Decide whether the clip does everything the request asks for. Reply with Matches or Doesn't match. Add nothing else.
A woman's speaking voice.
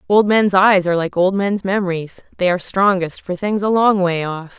Matches